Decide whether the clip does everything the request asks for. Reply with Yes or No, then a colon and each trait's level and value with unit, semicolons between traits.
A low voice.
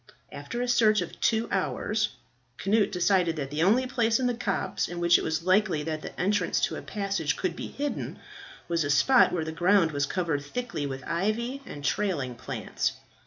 No: medium, 185 Hz